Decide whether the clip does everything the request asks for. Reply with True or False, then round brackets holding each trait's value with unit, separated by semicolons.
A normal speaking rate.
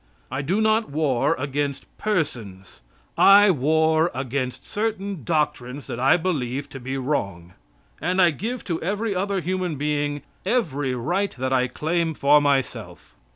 True (145 wpm)